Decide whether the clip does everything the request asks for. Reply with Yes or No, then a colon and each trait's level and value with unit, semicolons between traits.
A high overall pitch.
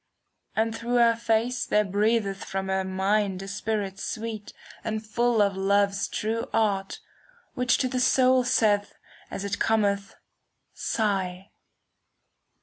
Yes: high, 210 Hz